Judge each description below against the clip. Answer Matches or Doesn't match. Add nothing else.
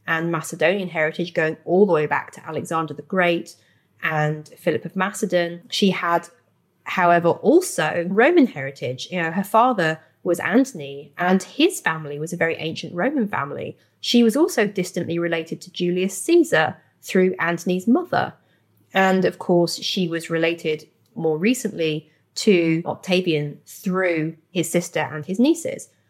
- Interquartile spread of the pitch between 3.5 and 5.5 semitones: Doesn't match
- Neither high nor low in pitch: Matches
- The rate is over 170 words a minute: Doesn't match